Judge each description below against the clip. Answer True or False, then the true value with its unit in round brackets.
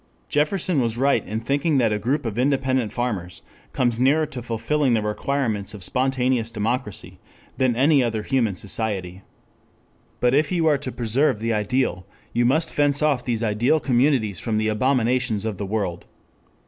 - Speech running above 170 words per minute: False (165 wpm)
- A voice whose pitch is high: False (120 Hz)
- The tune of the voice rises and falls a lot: False (4.0 semitones)